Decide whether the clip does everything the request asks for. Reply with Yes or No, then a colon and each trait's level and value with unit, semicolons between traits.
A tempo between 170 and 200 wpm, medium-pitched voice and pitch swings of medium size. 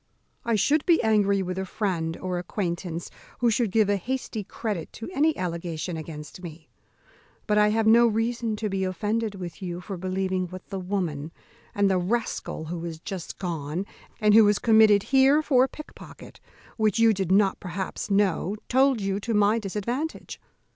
No: average, 175 wpm; high, 200 Hz; average, 3.7 semitones